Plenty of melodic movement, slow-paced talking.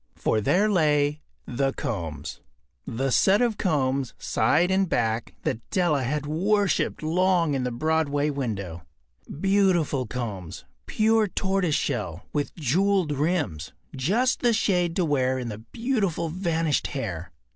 Yes: wide, 6.7 semitones; slow, 125 wpm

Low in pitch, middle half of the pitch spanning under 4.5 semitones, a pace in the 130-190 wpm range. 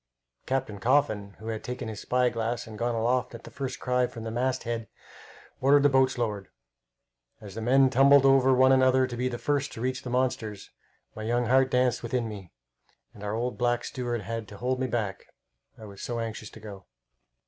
No: low, 120 Hz; narrow, 2.6 semitones; average, 200 wpm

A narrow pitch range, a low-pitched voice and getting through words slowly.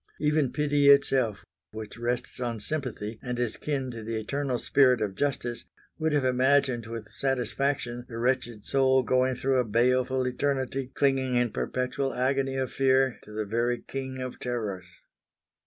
No: narrow, 2.2 semitones; low, 130 Hz; average, 155 wpm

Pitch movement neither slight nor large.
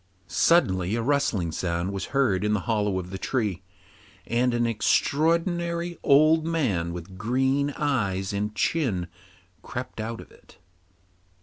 No: wide, 6.8 semitones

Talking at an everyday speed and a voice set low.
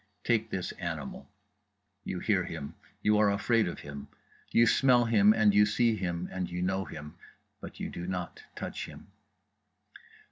Yes: average, 150 wpm; very low, 95 Hz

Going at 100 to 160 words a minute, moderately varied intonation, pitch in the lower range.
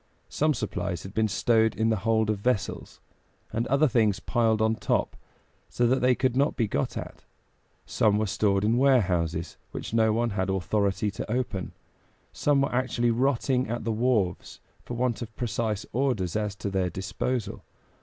No: average, 175 wpm; average, 3.5 semitones; low, 110 Hz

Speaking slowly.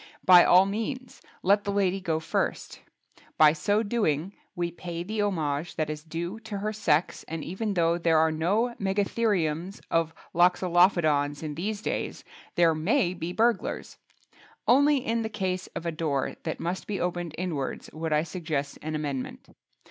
No: average, 160 wpm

